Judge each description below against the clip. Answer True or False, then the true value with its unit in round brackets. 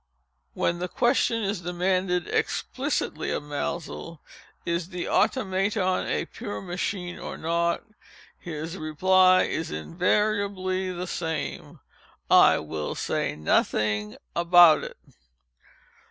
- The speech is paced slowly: True (95 wpm)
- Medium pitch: True (175 Hz)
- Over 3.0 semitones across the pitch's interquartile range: False (2.5 semitones)